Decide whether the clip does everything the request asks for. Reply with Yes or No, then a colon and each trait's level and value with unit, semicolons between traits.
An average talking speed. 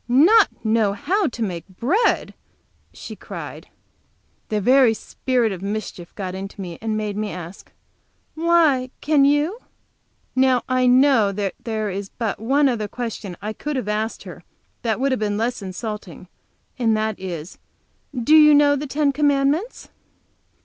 Yes: average, 145 wpm